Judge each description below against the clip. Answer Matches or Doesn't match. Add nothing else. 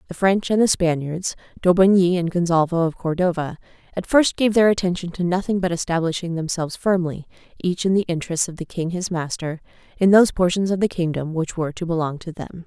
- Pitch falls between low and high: Matches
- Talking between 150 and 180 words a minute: Doesn't match